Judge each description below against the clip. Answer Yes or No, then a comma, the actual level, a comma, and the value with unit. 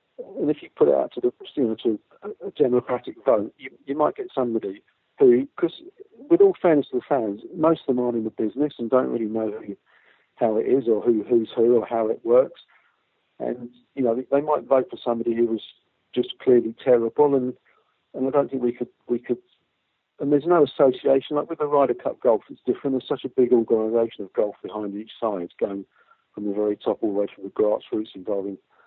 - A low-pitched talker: Yes, low, 125 Hz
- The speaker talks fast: Yes, fast, 220 wpm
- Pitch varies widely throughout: Yes, wide, 6.1 semitones